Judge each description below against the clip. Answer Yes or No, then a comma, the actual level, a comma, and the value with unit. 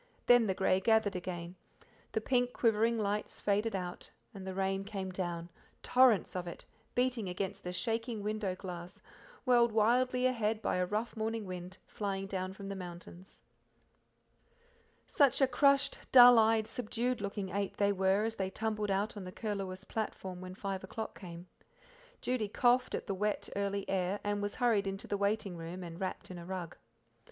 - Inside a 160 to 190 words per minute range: Yes, average, 175 wpm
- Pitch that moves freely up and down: No, average, 3.2 semitones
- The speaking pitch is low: No, high, 200 Hz